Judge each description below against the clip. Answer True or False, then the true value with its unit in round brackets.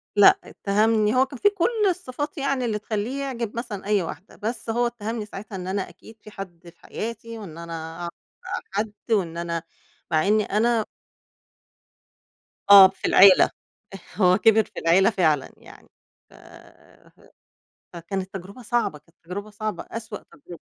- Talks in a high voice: True (210 Hz)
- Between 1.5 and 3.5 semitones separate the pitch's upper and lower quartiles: False (4.0 semitones)